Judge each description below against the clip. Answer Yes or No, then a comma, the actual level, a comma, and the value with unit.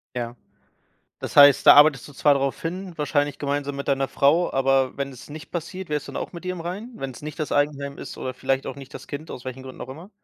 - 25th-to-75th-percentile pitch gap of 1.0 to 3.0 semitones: Yes, narrow, 2.6 semitones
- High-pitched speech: No, medium, 145 Hz